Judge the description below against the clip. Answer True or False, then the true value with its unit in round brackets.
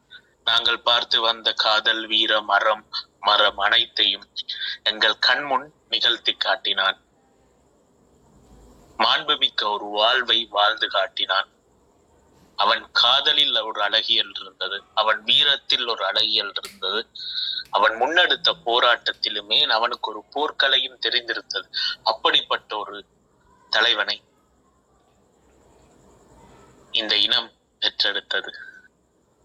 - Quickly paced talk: False (80 wpm)